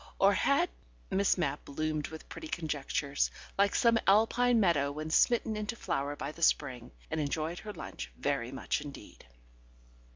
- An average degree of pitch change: No, wide, 6.5 semitones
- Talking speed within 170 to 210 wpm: No, average, 155 wpm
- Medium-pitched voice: Yes, medium, 160 Hz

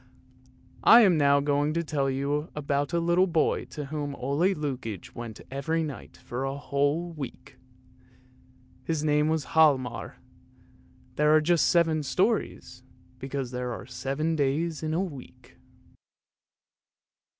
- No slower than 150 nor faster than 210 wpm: No, slow, 135 wpm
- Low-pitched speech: No, medium, 145 Hz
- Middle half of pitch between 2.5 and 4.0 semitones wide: Yes, average, 2.9 semitones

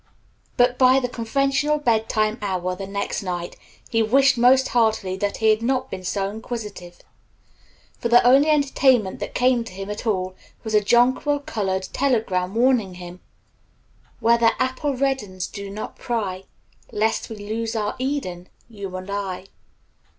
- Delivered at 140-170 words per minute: Yes, average, 160 wpm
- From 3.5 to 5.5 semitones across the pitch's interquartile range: Yes, average, 4.5 semitones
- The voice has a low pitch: No, high, 220 Hz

